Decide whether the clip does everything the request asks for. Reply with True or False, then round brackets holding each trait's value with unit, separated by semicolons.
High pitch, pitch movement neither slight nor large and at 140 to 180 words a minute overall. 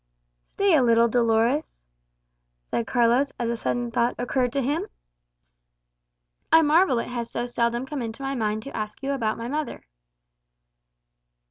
True (245 Hz; 3.0 semitones; 150 wpm)